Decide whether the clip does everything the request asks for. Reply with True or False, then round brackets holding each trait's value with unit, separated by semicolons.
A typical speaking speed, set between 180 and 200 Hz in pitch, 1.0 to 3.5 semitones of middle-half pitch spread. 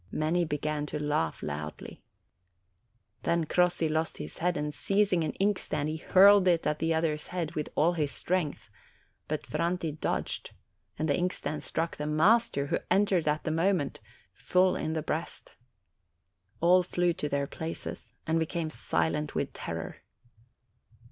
False (150 wpm; 160 Hz; 2.8 semitones)